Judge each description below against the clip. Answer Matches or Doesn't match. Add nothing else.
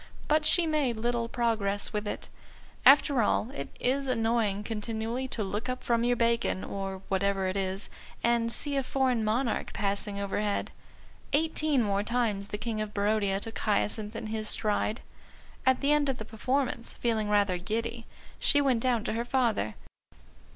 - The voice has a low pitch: Doesn't match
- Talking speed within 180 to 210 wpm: Doesn't match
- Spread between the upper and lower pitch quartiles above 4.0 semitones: Doesn't match